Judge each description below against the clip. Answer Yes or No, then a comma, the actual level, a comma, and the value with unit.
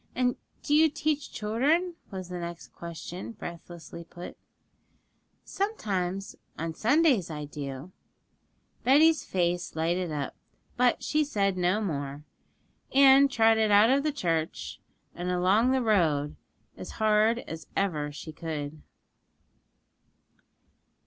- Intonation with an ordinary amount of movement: No, wide, 7.3 semitones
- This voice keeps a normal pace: No, slow, 115 wpm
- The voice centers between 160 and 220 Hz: Yes, medium, 185 Hz